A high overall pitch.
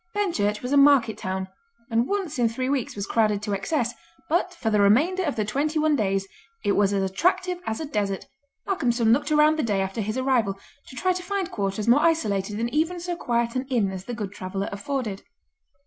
Yes: high, 235 Hz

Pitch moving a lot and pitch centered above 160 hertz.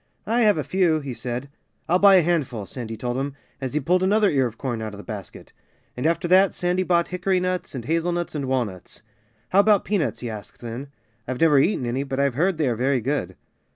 No: wide, 6.6 semitones; medium, 140 Hz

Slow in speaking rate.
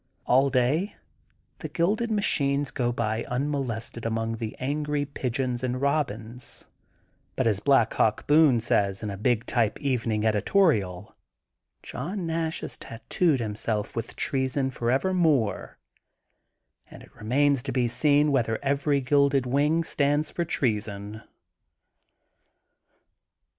Yes: slow, 125 wpm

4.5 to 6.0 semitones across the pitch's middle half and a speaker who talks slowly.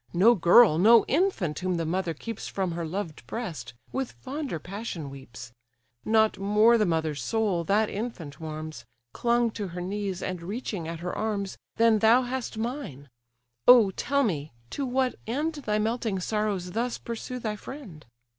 No: wide, 5.6 semitones; average, 165 wpm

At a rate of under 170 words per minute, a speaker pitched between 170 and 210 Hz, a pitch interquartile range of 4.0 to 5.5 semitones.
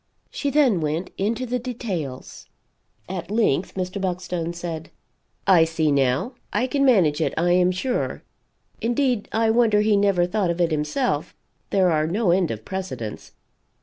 Yes: average, 155 wpm; medium, 185 Hz; average, 5.2 semitones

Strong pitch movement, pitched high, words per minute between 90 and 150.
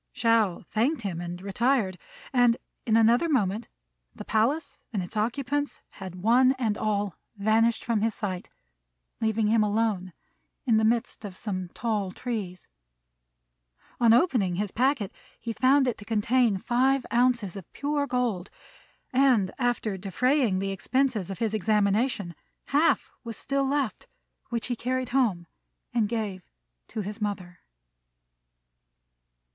No: average, 3.9 semitones; high, 225 Hz; slow, 135 wpm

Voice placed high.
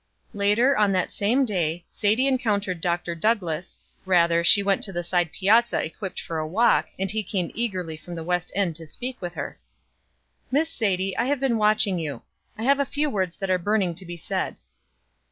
Yes: high, 195 Hz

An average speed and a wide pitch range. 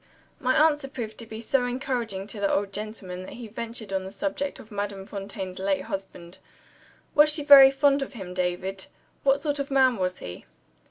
Yes: average, 195 wpm; wide, 5.9 semitones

